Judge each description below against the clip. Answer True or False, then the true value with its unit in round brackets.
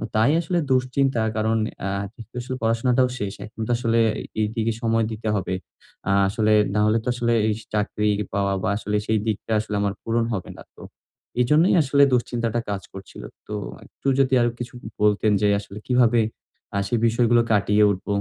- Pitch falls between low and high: False (115 Hz)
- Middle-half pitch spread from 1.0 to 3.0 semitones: True (2.5 semitones)